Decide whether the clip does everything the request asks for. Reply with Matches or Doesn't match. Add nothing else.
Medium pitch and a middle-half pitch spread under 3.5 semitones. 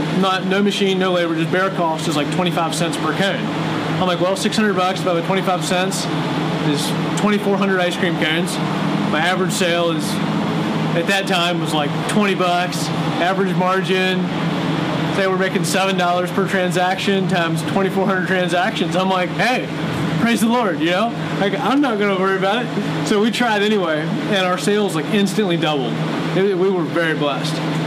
Matches